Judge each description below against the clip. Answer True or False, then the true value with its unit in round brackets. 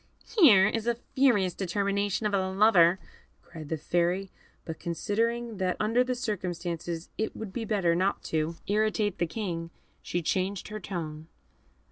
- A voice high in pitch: True (195 Hz)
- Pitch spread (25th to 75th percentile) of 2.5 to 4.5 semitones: True (3.9 semitones)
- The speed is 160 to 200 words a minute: False (150 wpm)